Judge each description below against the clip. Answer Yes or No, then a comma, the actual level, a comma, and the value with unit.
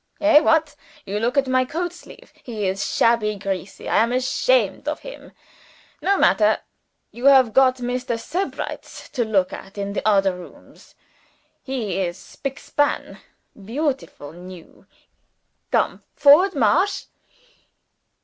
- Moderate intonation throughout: No, wide, 6.3 semitones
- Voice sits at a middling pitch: No, high, 245 Hz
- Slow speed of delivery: Yes, slow, 130 wpm